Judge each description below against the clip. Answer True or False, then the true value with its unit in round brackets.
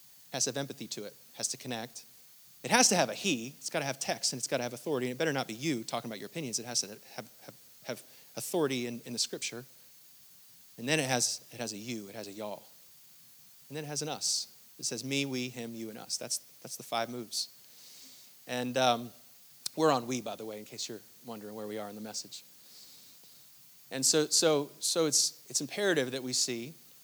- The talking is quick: True (235 wpm)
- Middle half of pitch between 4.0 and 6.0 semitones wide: False (3.3 semitones)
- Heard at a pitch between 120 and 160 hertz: True (125 Hz)